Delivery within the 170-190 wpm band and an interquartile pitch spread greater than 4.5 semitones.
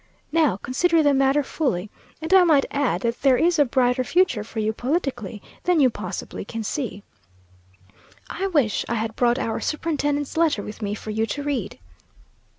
Yes: average, 175 wpm; average, 5.3 semitones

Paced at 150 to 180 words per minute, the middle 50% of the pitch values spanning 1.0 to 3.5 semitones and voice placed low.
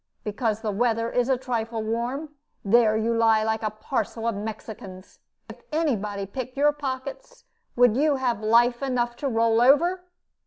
No: average, 165 wpm; average, 3.1 semitones; high, 235 Hz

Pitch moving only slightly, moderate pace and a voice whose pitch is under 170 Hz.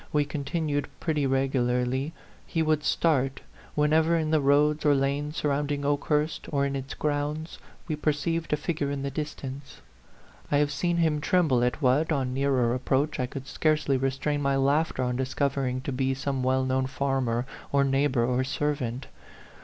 Yes: narrow, 2.2 semitones; average, 175 wpm; medium, 140 Hz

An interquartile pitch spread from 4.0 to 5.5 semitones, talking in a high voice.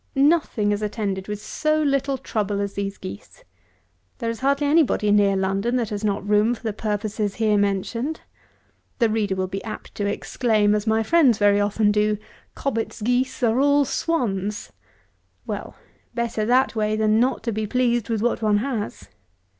No: average, 3.1 semitones; high, 215 Hz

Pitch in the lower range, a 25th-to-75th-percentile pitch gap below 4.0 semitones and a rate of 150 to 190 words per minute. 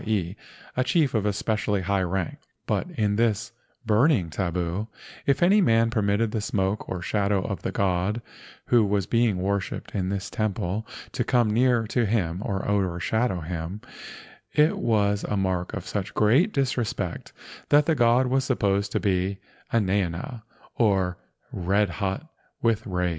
Yes: low, 105 Hz; average, 3.5 semitones; average, 155 wpm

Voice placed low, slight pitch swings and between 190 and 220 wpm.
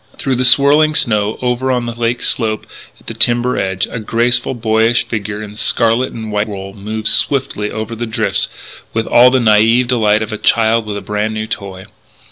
Yes: low, 110 Hz; narrow, 2.3 semitones; average, 195 wpm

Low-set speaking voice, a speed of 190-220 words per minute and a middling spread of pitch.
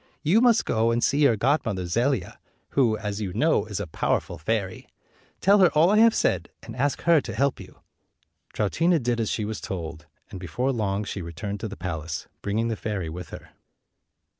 No: low, 110 Hz; average, 200 wpm; wide, 6.6 semitones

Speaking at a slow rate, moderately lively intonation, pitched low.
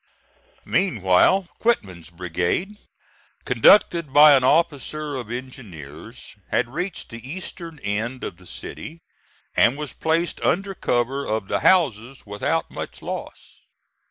No: slow, 120 wpm; wide, 8.2 semitones; low, 130 Hz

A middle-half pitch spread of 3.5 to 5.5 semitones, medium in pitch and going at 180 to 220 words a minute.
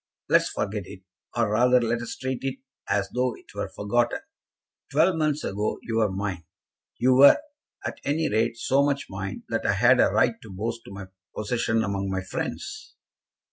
No: average, 3.8 semitones; low, 115 Hz; average, 185 wpm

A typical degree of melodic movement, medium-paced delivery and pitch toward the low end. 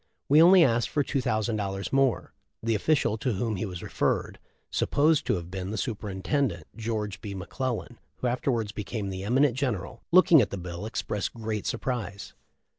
Yes: average, 4.7 semitones; average, 180 wpm; low, 110 Hz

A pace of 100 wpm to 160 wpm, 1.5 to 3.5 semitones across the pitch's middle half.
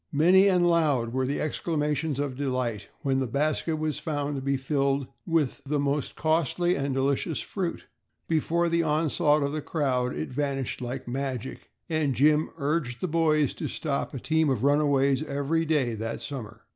No: average, 170 wpm; average, 2.9 semitones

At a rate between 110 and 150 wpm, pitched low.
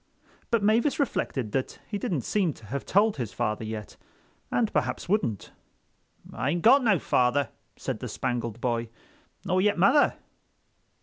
No: average, 145 wpm; medium, 145 Hz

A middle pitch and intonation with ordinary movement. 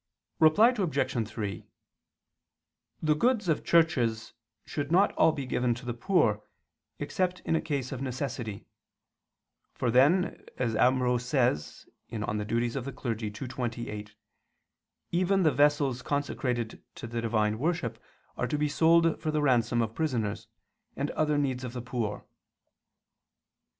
No: low, 130 Hz; average, 4.8 semitones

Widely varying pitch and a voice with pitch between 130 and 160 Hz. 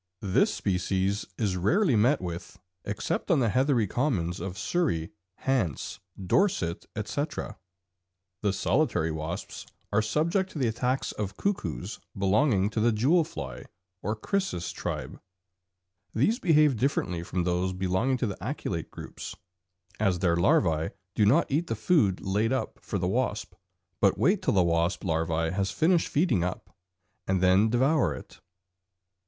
No: wide, 6.6 semitones; low, 105 Hz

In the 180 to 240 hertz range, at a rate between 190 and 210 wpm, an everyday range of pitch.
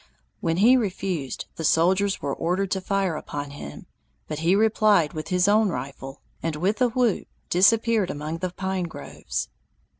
No: medium, 185 Hz; average, 160 wpm; average, 4.0 semitones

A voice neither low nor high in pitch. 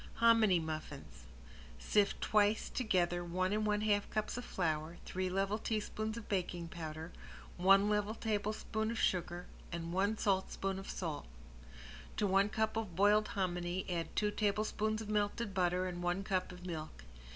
No: high, 195 Hz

